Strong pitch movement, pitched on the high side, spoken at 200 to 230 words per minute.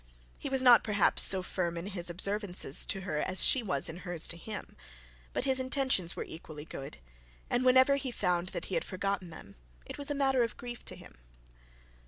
Yes: wide, 6.7 semitones; high, 195 Hz; fast, 205 wpm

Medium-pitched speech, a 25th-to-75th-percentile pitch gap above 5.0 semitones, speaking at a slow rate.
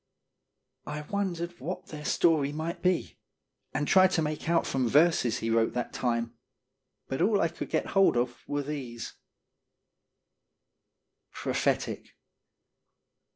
Yes: medium, 150 Hz; wide, 5.4 semitones; slow, 125 wpm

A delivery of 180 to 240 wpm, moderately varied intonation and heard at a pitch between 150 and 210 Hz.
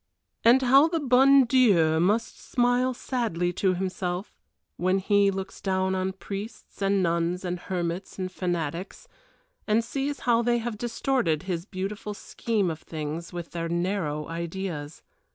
No: average, 145 wpm; average, 5.0 semitones; high, 190 Hz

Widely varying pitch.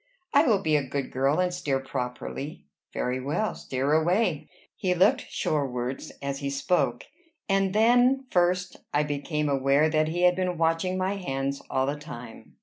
No: average, 5.0 semitones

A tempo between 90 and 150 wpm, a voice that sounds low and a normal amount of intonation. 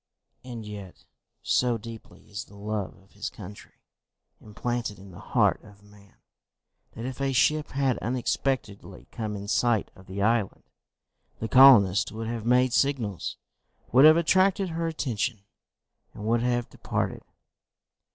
Yes: average, 140 wpm; low, 115 Hz; average, 3.9 semitones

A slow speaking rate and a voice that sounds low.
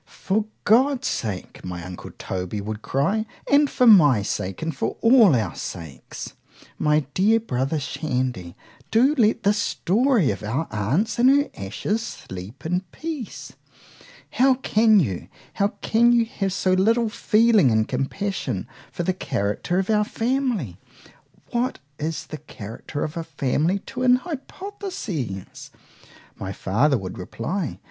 No: slow, 130 wpm; medium, 180 Hz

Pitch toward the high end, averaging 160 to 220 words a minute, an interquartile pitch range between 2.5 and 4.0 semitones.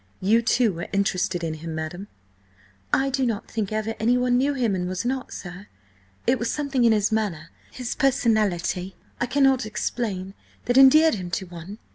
No: high, 220 Hz; average, 165 wpm; average, 5.2 semitones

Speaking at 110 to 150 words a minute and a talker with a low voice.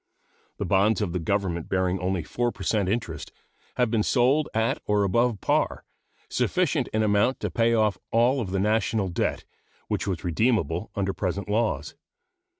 No: average, 165 wpm; low, 105 Hz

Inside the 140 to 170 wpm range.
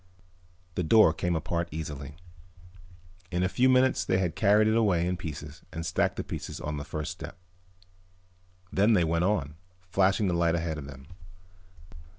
Yes: average, 165 wpm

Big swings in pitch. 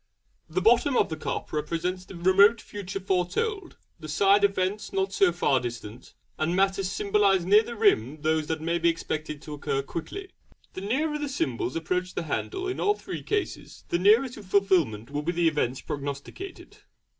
No: average, 4.8 semitones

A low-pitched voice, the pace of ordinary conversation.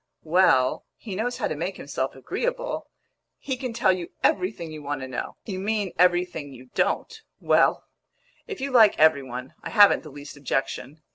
No: medium, 175 Hz; average, 180 wpm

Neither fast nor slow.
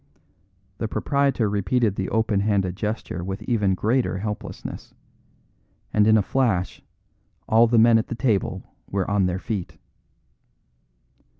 No: slow, 130 wpm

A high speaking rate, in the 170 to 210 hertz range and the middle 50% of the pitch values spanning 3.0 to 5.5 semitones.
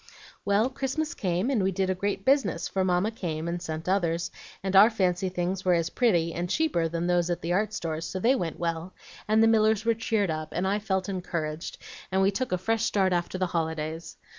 Yes: fast, 220 wpm; medium, 185 Hz; average, 3.9 semitones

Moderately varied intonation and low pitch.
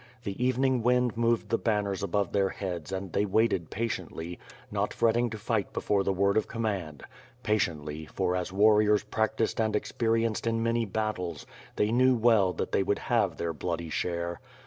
Yes: average, 3.7 semitones; low, 105 Hz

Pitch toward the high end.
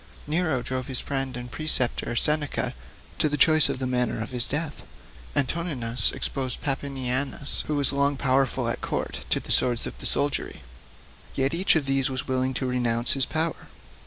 No: low, 135 Hz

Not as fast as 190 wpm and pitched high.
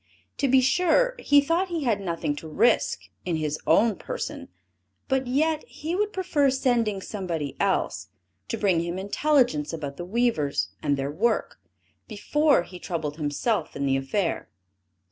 Yes: average, 155 wpm; high, 215 Hz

